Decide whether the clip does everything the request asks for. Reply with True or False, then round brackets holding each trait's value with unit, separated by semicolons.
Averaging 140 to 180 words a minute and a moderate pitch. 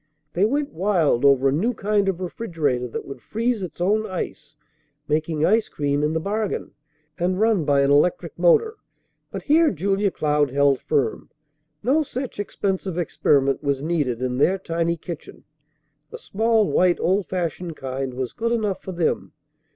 True (165 wpm; 175 Hz)